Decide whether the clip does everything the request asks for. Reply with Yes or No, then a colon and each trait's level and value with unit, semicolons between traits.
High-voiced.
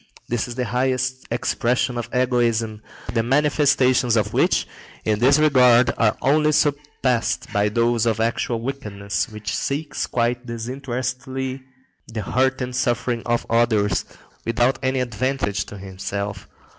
No: low, 120 Hz